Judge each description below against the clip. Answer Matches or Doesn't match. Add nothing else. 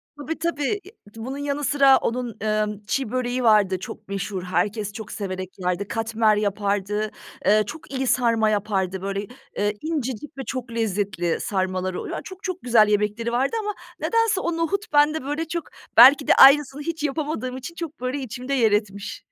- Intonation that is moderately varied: Doesn't match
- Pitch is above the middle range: Matches